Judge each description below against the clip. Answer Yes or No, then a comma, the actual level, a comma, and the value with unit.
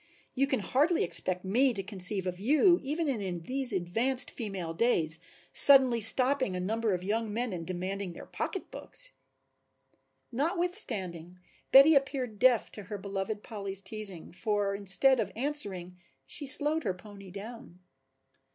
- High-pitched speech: Yes, high, 210 Hz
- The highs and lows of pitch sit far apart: Yes, wide, 6.0 semitones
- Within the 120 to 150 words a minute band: Yes, average, 140 wpm